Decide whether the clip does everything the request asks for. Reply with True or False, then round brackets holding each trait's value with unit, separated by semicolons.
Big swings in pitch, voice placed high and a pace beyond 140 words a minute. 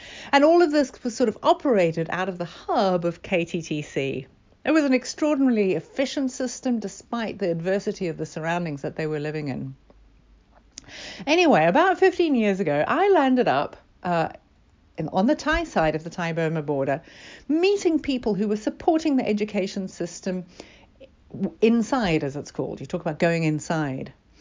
True (8.8 semitones; 195 Hz; 165 wpm)